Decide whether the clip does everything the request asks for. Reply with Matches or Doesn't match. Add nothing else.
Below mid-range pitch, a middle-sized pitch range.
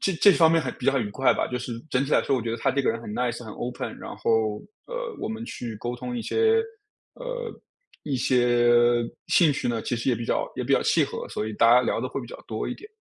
Matches